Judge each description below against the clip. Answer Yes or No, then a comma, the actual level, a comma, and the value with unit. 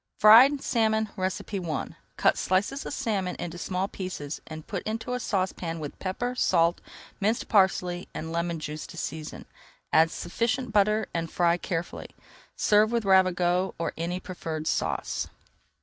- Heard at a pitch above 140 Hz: Yes, medium, 185 Hz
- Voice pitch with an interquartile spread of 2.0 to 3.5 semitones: No, average, 4.2 semitones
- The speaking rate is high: No, average, 150 wpm